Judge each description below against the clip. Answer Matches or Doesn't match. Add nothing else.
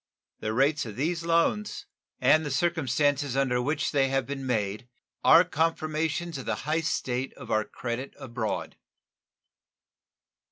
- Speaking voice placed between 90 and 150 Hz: Matches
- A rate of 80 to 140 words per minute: Matches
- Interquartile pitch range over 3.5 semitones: Matches